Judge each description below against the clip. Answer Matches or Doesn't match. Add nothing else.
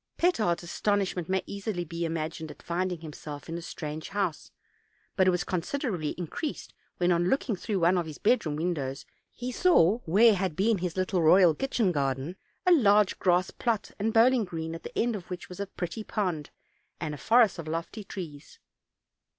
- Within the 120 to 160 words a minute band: Doesn't match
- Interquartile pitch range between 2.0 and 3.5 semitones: Doesn't match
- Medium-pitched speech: Matches